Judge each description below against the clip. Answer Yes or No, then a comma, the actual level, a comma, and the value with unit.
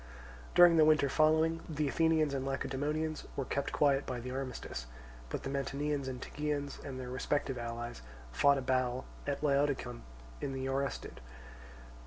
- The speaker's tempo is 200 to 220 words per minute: No, average, 155 wpm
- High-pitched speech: No, medium, 140 Hz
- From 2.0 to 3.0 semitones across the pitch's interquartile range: Yes, narrow, 2.4 semitones